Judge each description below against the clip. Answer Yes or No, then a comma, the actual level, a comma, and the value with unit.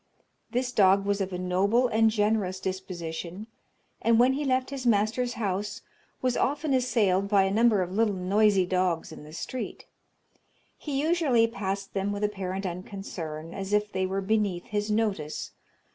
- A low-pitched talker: No, high, 205 Hz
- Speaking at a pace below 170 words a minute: Yes, average, 160 wpm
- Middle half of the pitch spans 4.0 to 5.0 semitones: No, average, 3.4 semitones